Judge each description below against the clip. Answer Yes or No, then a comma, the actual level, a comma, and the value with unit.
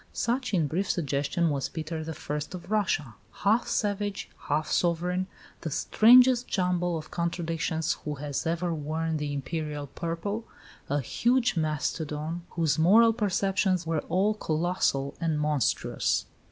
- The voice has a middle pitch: Yes, medium, 165 Hz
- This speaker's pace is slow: Yes, slow, 130 wpm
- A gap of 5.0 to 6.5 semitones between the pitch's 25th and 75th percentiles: No, average, 4.1 semitones